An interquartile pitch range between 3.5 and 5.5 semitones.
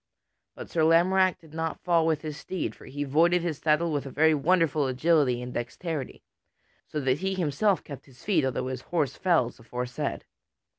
Yes: average, 4.2 semitones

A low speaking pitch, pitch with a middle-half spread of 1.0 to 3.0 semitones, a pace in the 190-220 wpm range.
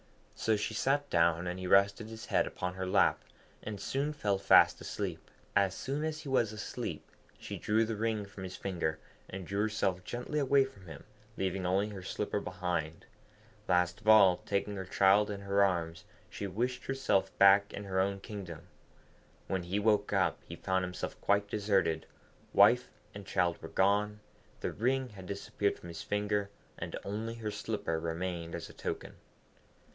No: low, 100 Hz; average, 2.7 semitones; average, 175 wpm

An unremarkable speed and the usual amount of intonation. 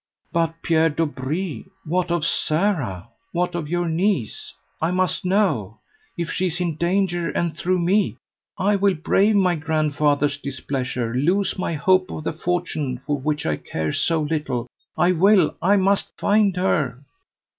Yes: average, 155 wpm; average, 3.9 semitones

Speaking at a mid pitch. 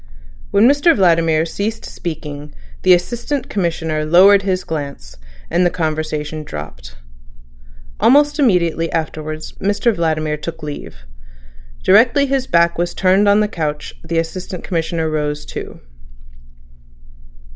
Yes: medium, 170 Hz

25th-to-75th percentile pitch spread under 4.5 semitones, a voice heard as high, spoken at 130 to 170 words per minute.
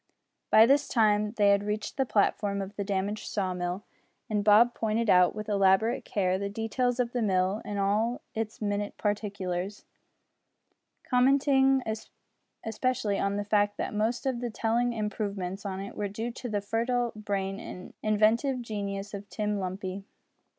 Yes: narrow, 2.4 semitones; high, 210 Hz; average, 160 wpm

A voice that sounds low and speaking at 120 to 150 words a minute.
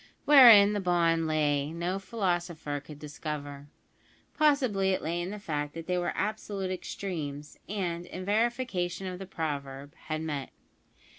No: medium, 175 Hz; average, 145 wpm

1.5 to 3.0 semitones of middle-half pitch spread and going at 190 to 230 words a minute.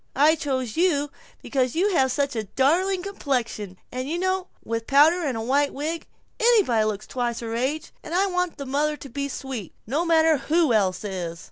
No: wide, 5.6 semitones; average, 195 wpm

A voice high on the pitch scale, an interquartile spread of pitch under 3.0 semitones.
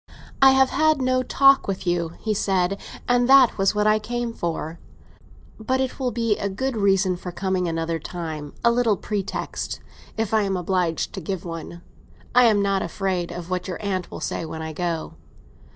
No: high, 195 Hz; average, 5.1 semitones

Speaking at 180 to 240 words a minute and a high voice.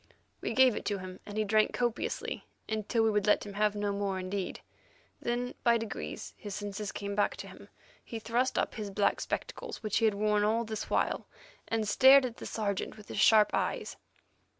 Yes: average, 200 wpm; high, 215 Hz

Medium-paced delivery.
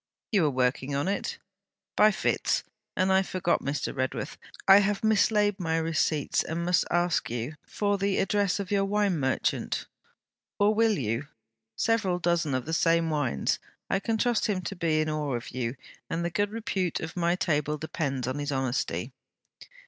Yes: average, 175 wpm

